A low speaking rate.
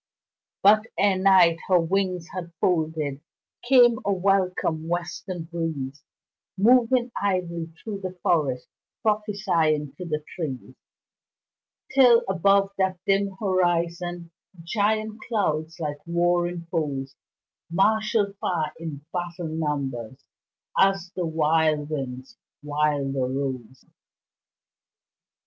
Yes: slow, 100 wpm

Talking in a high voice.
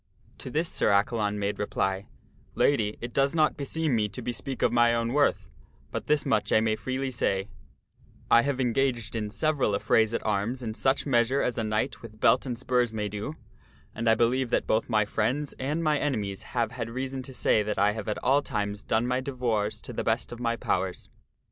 No: low, 115 Hz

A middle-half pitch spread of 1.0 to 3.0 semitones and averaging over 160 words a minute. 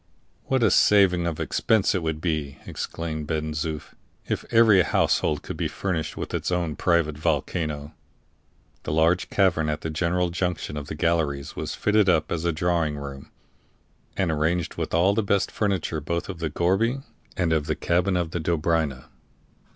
Yes: average, 2.7 semitones; average, 175 wpm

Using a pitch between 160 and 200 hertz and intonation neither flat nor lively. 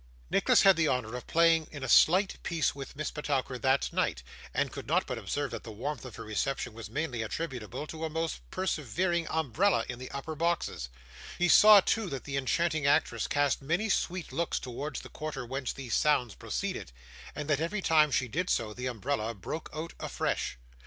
No: medium, 145 Hz; average, 4.6 semitones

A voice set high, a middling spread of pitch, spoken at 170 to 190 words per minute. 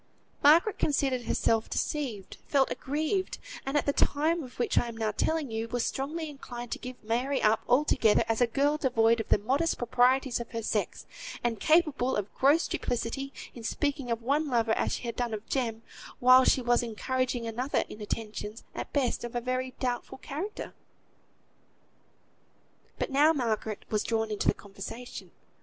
Yes: high, 245 Hz; average, 3.6 semitones; average, 175 wpm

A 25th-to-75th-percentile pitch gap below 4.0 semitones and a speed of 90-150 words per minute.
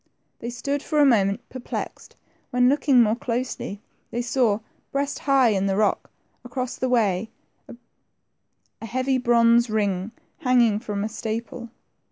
Yes: average, 2.9 semitones; average, 140 wpm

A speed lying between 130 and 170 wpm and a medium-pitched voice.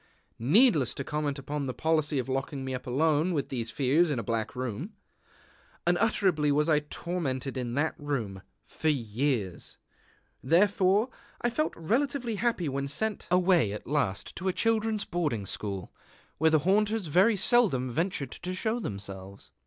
Yes: average, 155 wpm; medium, 150 Hz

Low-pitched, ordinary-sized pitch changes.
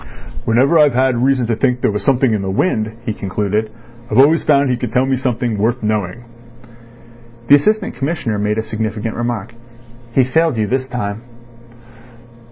Yes: low, 120 Hz; average, 3.6 semitones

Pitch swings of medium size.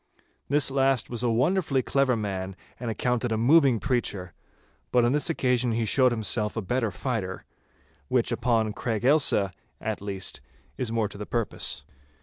Yes: average, 3.5 semitones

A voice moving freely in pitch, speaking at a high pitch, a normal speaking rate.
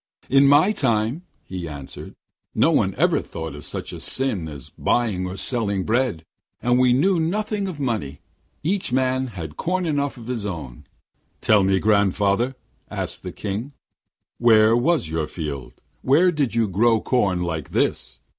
No: wide, 6.5 semitones; low, 115 Hz; average, 165 wpm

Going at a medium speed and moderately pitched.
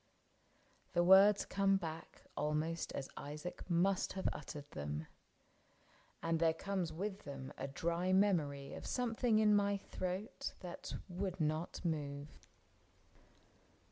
No: slow, 125 wpm; medium, 170 Hz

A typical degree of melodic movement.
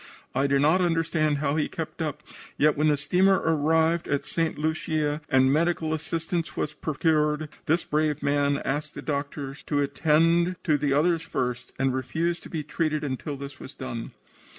No: narrow, 2.3 semitones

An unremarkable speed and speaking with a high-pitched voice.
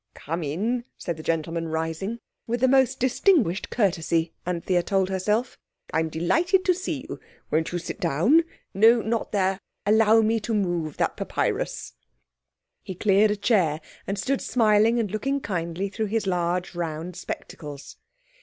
Yes: average, 155 wpm; high, 195 Hz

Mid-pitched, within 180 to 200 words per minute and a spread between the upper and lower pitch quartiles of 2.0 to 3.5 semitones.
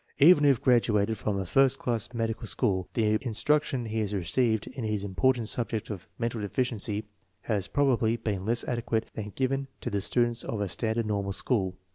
No: low, 115 Hz; average, 185 wpm; average, 3.1 semitones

